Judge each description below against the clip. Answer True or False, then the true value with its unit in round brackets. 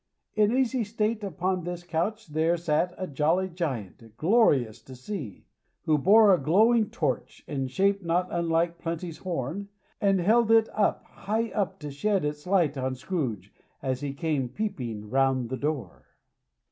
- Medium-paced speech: True (160 wpm)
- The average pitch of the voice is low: False (170 Hz)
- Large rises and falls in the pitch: True (6.5 semitones)